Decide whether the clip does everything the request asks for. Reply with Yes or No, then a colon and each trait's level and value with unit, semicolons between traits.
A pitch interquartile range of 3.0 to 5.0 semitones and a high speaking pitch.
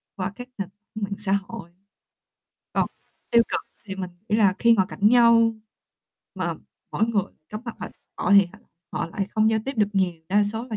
No: narrow, 2.6 semitones; high, 210 Hz